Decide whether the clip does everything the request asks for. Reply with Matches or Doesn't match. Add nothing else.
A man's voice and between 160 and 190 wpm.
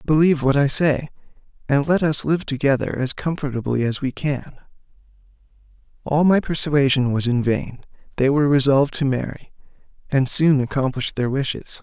Doesn't match